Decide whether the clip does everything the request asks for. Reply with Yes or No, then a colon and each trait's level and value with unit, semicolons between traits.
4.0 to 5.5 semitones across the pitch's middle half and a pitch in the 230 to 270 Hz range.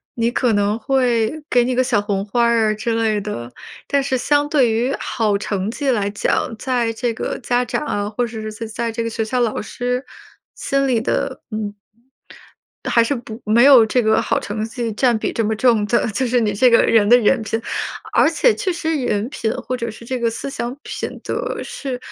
No: average, 2.7 semitones; high, 235 Hz